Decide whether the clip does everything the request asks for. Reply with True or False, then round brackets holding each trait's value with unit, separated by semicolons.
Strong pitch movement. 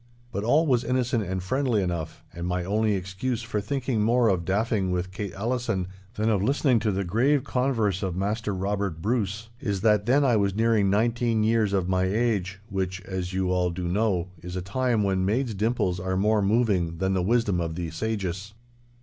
False (3.7 semitones)